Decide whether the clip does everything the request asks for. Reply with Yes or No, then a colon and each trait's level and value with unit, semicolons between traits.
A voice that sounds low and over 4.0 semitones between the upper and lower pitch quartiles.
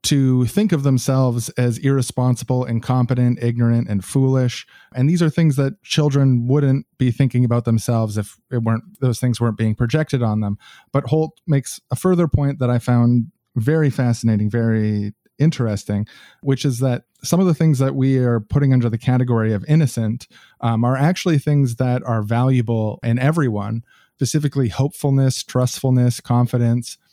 No: low, 125 Hz; average, 2.8 semitones